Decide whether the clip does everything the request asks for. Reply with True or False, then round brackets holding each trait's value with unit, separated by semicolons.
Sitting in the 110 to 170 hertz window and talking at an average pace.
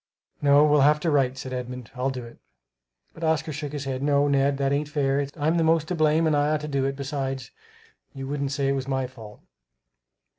False (140 Hz; 225 wpm)